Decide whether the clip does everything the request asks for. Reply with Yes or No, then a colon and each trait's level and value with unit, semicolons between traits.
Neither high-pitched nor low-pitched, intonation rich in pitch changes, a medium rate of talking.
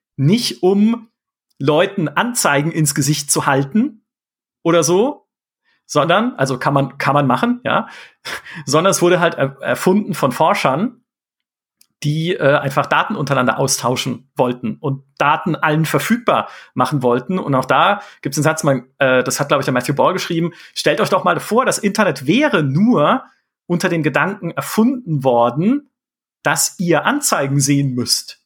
Yes: medium, 155 Hz; wide, 6.1 semitones; average, 155 wpm